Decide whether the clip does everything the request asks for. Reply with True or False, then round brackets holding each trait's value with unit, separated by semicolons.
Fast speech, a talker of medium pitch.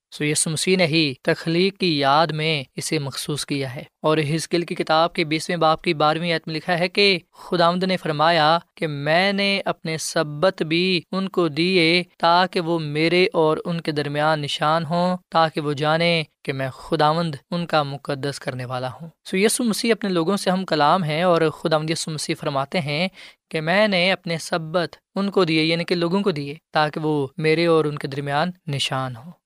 True (195 wpm; 165 Hz)